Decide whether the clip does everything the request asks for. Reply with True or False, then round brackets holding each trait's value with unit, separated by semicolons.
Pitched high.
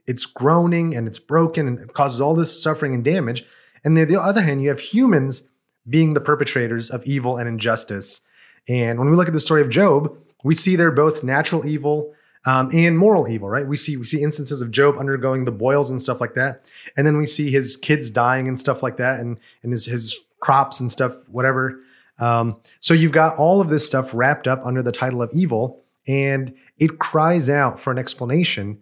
False (135 Hz)